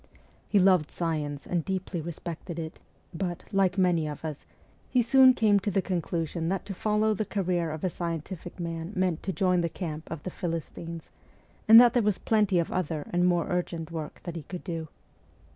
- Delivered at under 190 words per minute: No, average, 195 wpm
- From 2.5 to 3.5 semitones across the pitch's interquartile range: Yes, average, 2.9 semitones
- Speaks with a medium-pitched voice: Yes, medium, 175 Hz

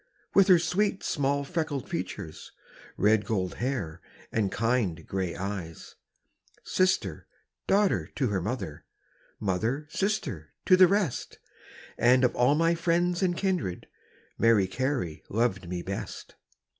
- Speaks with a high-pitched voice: No, low, 125 Hz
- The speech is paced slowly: Yes, slow, 125 wpm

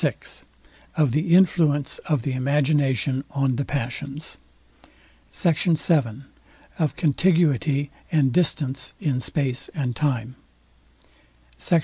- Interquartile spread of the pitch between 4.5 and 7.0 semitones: No, average, 3.2 semitones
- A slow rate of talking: Yes, slow, 105 wpm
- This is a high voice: No, medium, 140 Hz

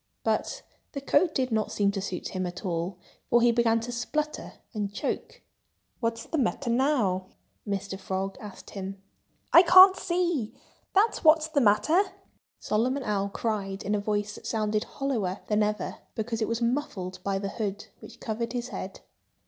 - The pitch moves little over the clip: No, average, 5.0 semitones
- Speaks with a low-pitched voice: No, high, 220 Hz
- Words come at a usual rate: Yes, average, 165 wpm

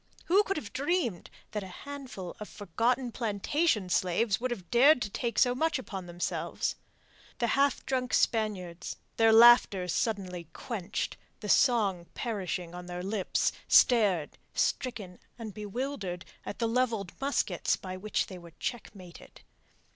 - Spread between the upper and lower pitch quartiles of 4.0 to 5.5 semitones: Yes, average, 5.2 semitones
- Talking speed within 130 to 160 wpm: Yes, average, 140 wpm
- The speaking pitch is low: No, high, 215 Hz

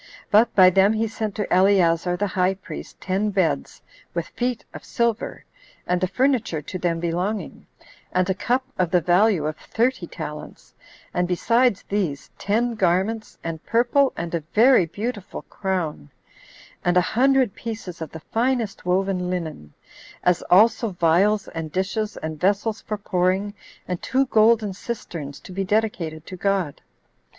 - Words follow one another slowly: No, average, 155 wpm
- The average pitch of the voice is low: No, high, 190 Hz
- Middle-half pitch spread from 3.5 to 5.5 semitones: Yes, average, 4.1 semitones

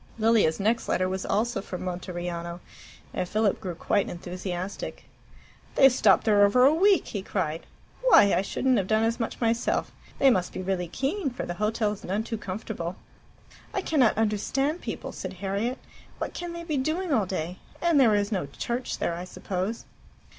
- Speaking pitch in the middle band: No, high, 210 Hz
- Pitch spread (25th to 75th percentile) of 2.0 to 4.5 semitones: No, average, 5.1 semitones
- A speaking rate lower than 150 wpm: No, average, 175 wpm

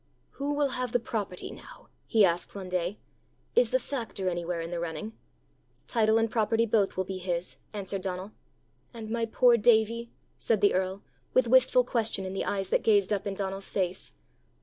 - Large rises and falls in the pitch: No, average, 3.7 semitones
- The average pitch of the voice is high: Yes, high, 205 Hz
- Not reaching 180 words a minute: No, average, 185 wpm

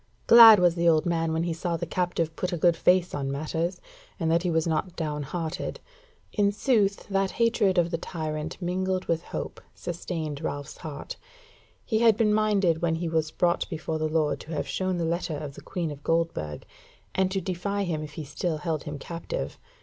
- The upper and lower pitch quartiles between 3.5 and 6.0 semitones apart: No, average, 2.9 semitones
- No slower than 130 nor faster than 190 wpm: No, fast, 205 wpm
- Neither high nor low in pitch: Yes, medium, 170 Hz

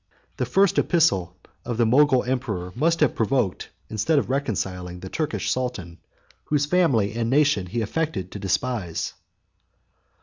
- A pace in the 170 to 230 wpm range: No, average, 145 wpm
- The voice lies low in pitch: Yes, low, 120 Hz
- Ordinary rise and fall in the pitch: No, wide, 7.2 semitones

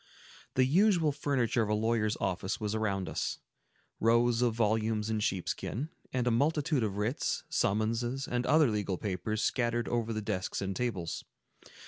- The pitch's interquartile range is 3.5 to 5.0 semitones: No, average, 2.7 semitones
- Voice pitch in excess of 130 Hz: No, low, 115 Hz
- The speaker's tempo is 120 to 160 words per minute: Yes, average, 150 wpm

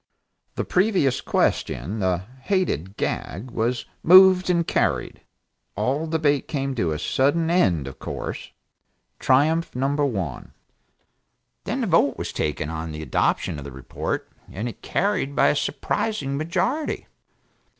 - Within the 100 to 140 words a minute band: Yes, slow, 135 wpm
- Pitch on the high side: No, medium, 140 Hz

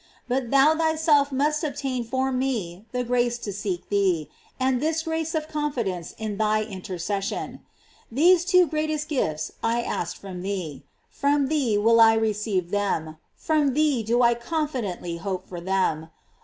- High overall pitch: Yes, high, 235 Hz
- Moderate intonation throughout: No, wide, 6.9 semitones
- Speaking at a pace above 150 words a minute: Yes, average, 160 wpm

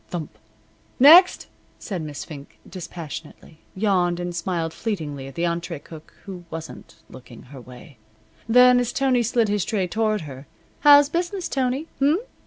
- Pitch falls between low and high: Yes, medium, 180 Hz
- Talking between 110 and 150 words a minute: Yes, average, 145 wpm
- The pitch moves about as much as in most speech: No, wide, 7.7 semitones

